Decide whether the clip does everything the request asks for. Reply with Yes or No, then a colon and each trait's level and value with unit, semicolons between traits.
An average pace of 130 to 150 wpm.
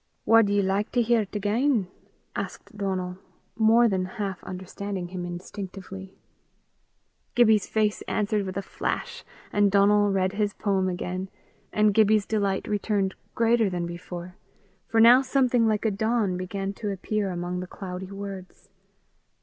Yes: average, 145 wpm